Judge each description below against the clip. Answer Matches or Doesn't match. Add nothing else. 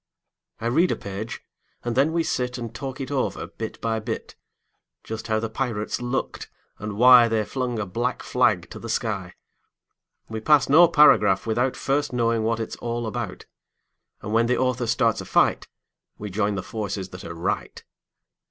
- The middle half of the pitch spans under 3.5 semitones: Matches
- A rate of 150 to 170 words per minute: Doesn't match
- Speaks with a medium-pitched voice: Doesn't match